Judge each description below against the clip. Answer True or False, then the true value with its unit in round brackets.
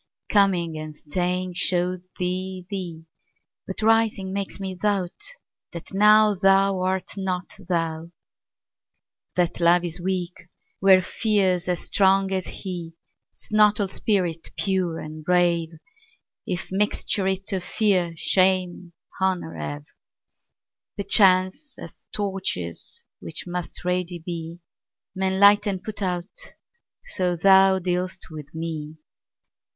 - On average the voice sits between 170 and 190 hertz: True (185 Hz)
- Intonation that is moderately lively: False (2.1 semitones)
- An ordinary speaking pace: False (105 wpm)